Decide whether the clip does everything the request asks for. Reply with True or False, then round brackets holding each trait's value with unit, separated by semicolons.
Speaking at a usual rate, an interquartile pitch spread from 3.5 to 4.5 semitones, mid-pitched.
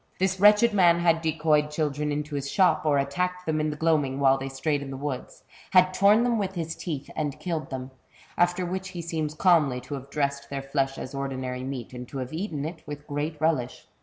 False (220 wpm; 4.0 semitones; 150 Hz)